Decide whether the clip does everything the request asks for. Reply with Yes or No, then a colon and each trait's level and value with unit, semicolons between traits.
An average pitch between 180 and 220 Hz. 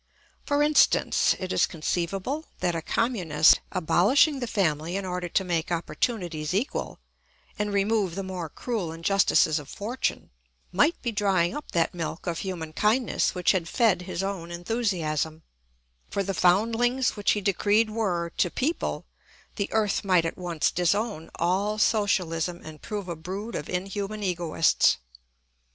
Yes: high, 190 Hz